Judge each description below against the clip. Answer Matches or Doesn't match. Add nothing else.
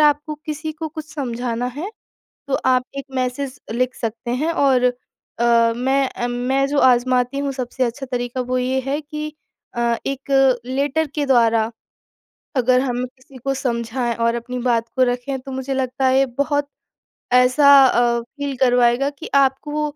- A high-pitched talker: Matches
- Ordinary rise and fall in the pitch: Doesn't match